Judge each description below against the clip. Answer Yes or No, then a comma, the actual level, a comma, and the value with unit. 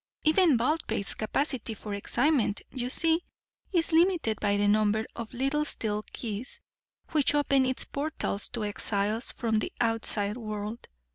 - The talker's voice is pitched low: No, high, 235 Hz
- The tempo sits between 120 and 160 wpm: Yes, average, 140 wpm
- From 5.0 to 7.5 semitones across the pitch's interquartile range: Yes, wide, 5.6 semitones